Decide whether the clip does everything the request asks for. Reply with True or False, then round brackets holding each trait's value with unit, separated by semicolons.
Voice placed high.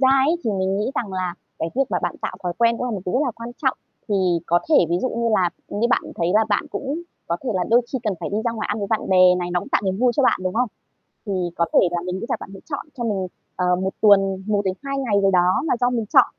True (205 Hz)